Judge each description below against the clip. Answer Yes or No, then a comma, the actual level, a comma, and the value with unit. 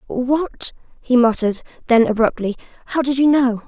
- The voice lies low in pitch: No, very high, 250 Hz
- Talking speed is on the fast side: No, average, 145 wpm